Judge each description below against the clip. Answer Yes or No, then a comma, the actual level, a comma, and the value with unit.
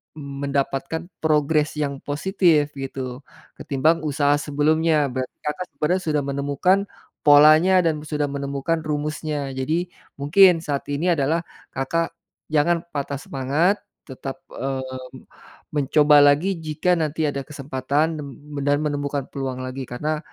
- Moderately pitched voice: Yes, medium, 145 Hz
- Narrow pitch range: Yes, narrow, 2.3 semitones